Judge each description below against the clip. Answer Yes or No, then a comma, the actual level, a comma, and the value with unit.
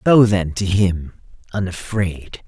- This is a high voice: No, very low, 95 Hz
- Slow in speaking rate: Yes, slow, 95 wpm